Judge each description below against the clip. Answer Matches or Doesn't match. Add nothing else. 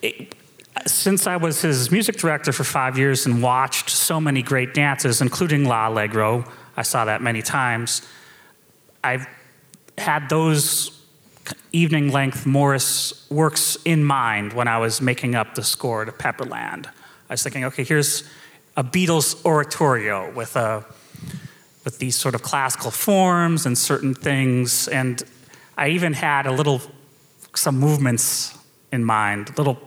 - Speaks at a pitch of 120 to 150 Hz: Matches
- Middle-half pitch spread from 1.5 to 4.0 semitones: Matches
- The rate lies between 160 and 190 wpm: Doesn't match